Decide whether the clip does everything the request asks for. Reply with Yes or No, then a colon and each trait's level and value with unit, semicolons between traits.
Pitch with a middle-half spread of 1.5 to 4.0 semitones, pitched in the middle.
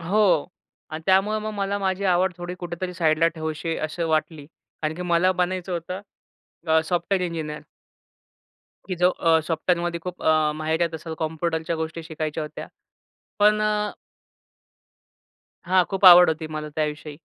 Yes: narrow, 2.5 semitones; medium, 170 Hz